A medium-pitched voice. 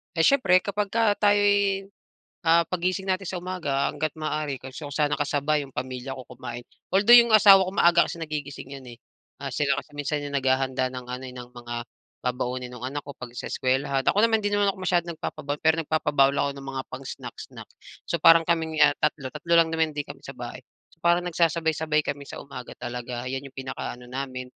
Yes: medium, 150 Hz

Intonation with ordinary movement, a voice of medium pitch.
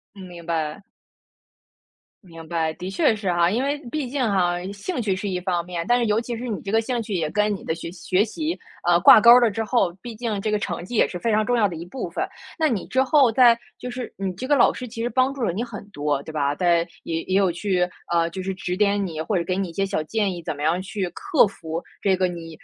No: average, 5.0 semitones; high, 195 Hz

